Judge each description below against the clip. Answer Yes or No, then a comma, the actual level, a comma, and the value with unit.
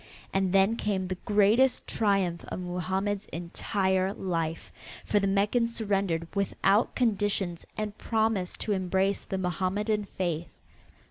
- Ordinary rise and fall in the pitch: No, narrow, 2.2 semitones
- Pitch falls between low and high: No, high, 195 Hz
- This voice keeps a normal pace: No, slow, 125 wpm